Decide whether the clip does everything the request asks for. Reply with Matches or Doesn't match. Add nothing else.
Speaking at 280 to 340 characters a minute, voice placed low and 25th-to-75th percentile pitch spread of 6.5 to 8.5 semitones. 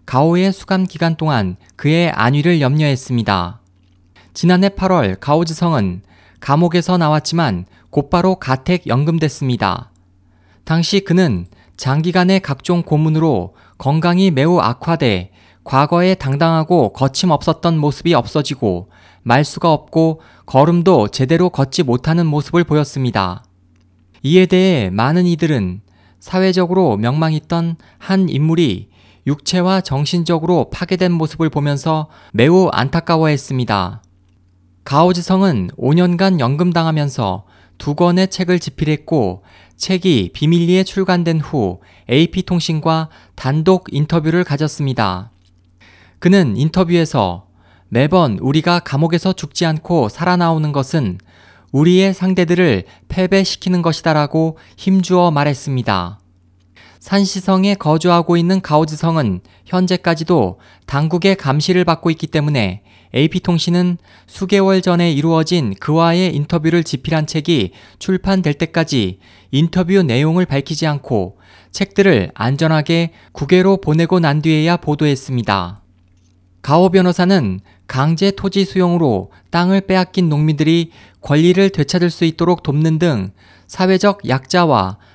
Doesn't match